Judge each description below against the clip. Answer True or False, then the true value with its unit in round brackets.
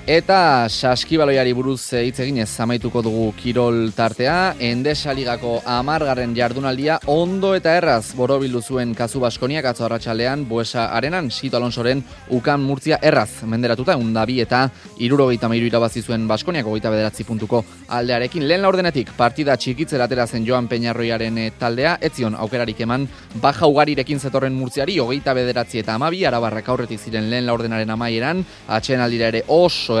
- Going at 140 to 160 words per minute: True (145 wpm)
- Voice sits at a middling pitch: False (125 Hz)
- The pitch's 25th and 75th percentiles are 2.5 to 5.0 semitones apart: True (2.9 semitones)